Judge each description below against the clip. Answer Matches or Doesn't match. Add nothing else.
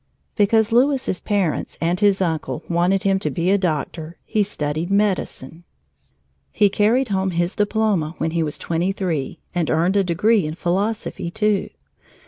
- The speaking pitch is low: Doesn't match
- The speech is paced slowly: Doesn't match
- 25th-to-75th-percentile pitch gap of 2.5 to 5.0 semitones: Matches